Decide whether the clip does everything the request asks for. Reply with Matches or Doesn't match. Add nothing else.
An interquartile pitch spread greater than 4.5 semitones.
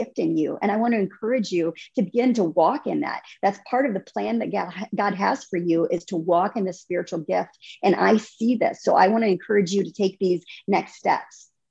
Doesn't match